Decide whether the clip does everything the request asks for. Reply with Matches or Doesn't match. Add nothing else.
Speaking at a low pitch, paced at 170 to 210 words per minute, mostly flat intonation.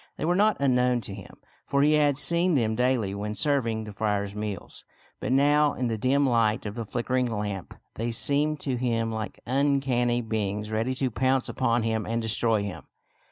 Doesn't match